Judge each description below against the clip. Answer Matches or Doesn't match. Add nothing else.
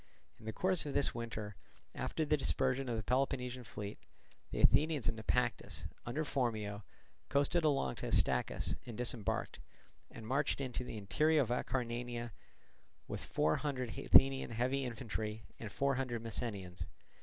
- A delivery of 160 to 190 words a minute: Doesn't match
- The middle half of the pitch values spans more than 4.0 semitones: Doesn't match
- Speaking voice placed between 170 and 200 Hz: Doesn't match